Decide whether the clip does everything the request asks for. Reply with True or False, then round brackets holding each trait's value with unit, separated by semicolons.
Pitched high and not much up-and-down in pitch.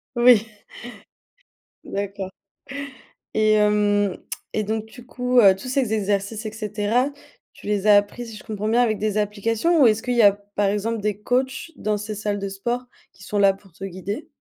True (210 Hz; 2.1 semitones)